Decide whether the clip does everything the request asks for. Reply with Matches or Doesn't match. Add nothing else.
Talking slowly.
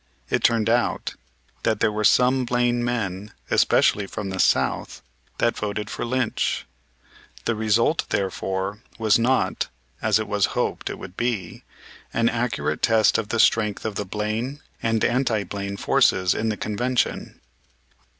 Doesn't match